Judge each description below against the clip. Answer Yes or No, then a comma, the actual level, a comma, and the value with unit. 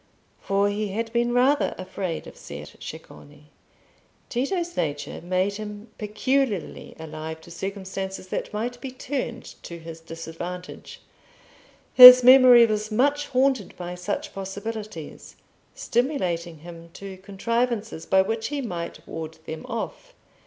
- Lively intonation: Yes, wide, 5.8 semitones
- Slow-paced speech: Yes, slow, 125 wpm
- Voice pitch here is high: Yes, high, 205 Hz